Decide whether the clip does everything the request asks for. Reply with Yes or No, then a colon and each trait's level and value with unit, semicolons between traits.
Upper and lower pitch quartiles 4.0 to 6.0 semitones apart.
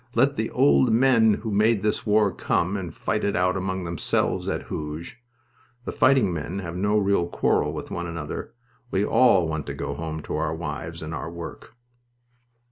Yes: average, 4.4 semitones